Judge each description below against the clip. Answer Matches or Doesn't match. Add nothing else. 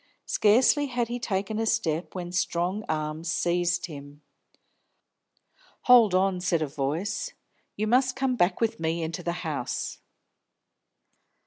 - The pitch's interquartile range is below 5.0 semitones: Doesn't match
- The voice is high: Doesn't match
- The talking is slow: Matches